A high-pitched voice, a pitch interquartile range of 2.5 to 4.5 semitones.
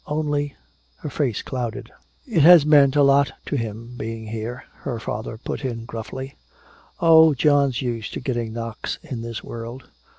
No: low, 125 Hz; average, 3.9 semitones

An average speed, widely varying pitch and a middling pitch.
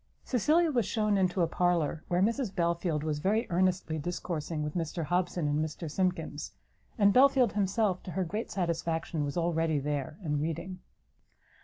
No: average, 160 wpm; average, 3.7 semitones; medium, 175 Hz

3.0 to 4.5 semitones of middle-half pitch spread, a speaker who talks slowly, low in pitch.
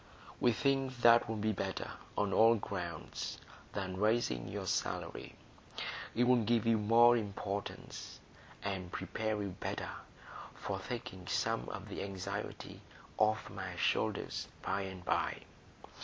Yes: average, 3.4 semitones; slow, 125 wpm; low, 105 Hz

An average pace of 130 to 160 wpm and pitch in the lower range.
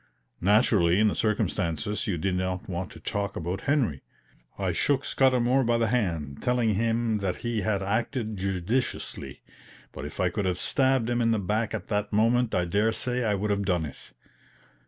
No: average, 185 wpm; low, 105 Hz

